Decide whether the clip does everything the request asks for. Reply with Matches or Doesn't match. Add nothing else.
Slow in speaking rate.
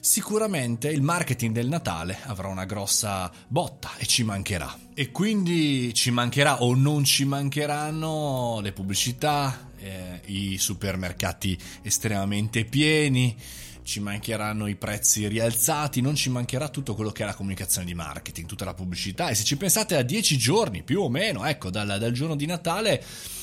Doesn't match